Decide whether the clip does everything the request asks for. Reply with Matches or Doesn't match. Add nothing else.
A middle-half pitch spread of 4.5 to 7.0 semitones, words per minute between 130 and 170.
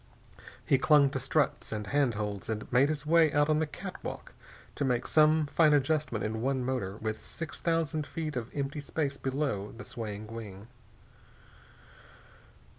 Matches